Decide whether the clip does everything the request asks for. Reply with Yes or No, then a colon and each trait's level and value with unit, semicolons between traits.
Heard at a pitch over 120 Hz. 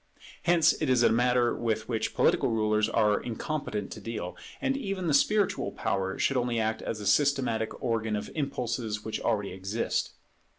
No: low, 115 Hz